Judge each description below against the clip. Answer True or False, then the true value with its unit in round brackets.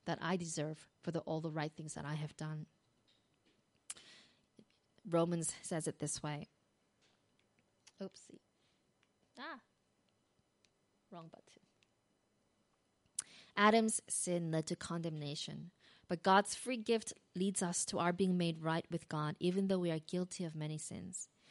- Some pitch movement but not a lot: True (3.0 semitones)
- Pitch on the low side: False (170 Hz)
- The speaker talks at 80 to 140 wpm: True (135 wpm)